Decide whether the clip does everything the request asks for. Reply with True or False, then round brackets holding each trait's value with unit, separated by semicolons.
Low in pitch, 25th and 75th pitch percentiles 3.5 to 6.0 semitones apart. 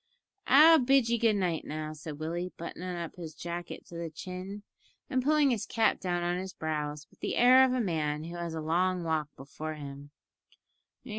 False (175 Hz; 5.0 semitones)